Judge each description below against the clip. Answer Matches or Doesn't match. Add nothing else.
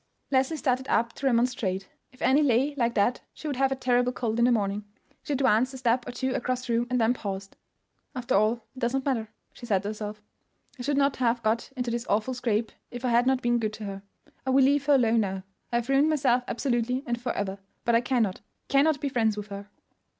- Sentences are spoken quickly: Matches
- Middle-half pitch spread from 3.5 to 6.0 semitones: Doesn't match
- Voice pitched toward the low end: Doesn't match